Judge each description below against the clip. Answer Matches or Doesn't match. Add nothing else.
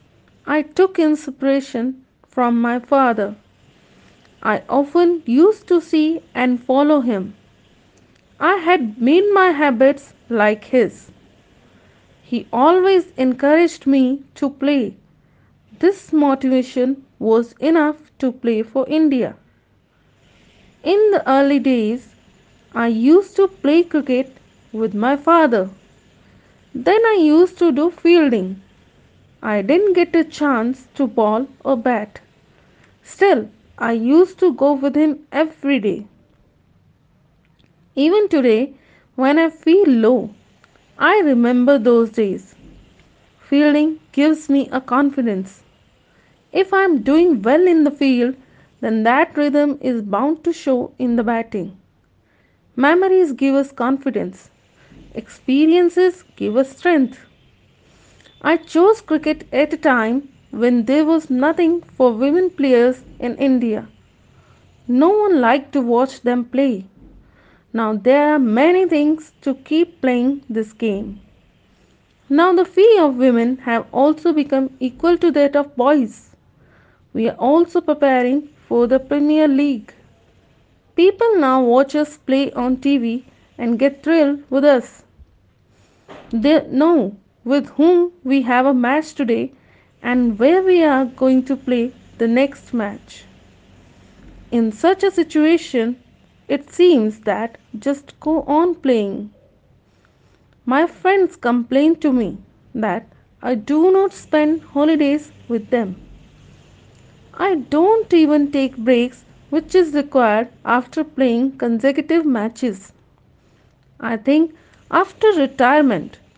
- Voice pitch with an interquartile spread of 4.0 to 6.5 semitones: Matches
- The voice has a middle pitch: Doesn't match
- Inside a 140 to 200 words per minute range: Doesn't match